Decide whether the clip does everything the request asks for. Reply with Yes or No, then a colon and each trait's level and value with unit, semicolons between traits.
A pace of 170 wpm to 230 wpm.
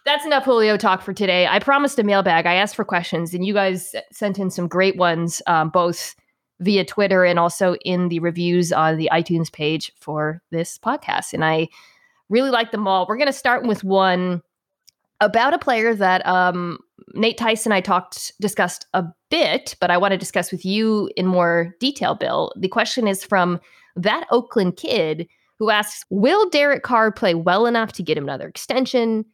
Yes: average, 190 wpm